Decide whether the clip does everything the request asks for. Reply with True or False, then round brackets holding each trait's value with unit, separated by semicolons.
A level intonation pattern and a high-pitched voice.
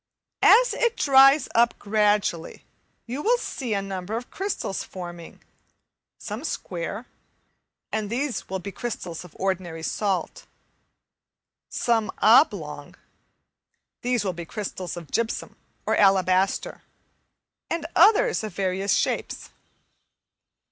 False (5.0 semitones; 210 Hz)